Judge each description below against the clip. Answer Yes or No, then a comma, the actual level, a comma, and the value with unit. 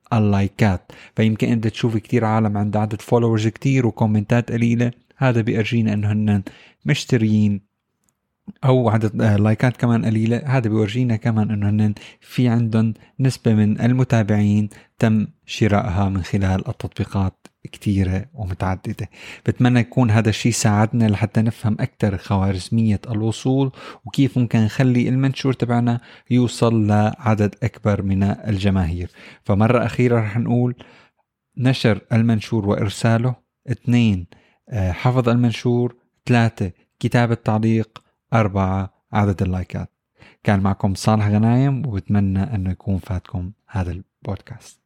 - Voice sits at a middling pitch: No, low, 110 Hz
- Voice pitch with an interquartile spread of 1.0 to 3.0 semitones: Yes, average, 2.7 semitones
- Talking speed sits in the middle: Yes, average, 110 wpm